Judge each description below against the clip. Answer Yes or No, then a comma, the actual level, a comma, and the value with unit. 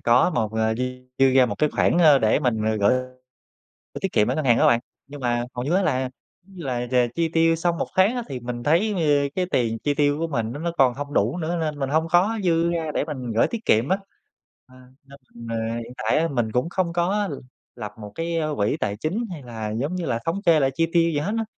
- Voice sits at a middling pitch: Yes, medium, 145 Hz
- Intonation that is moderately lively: No, wide, 5.7 semitones